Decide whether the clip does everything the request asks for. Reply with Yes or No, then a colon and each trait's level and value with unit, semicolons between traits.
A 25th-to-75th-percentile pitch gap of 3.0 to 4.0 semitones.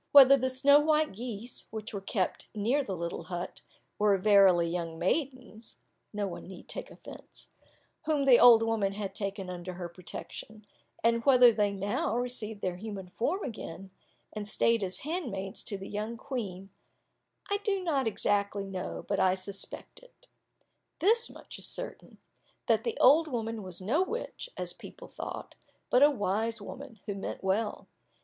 No: average, 4.9 semitones